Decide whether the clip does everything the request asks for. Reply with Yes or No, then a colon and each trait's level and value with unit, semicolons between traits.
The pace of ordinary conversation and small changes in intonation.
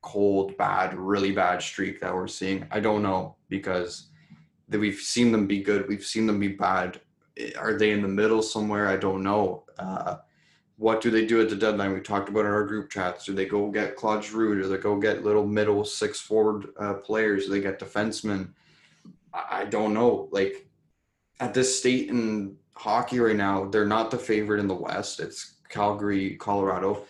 Yes: average, 195 wpm; narrow, 1.8 semitones